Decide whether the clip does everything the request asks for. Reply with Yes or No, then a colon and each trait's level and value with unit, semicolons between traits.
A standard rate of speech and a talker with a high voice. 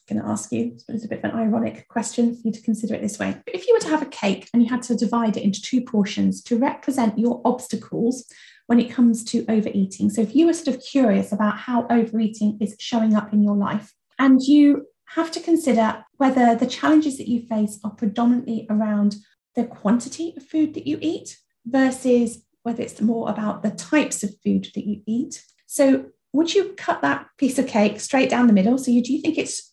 No: fast, 225 wpm; high, 235 Hz